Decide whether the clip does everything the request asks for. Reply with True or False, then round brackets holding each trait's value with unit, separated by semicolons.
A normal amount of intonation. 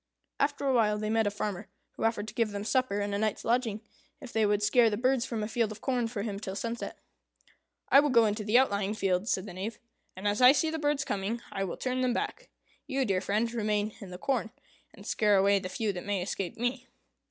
True (3.2 semitones)